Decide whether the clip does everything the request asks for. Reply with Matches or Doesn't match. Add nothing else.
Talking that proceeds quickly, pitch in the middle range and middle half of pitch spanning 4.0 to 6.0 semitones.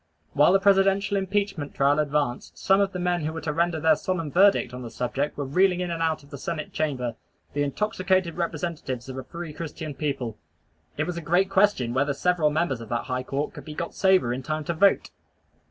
Matches